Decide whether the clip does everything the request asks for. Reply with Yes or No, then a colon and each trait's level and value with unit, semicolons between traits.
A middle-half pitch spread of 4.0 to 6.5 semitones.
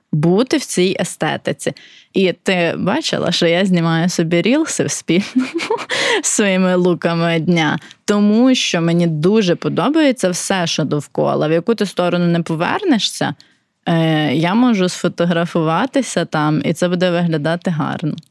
Yes: average, 4.4 semitones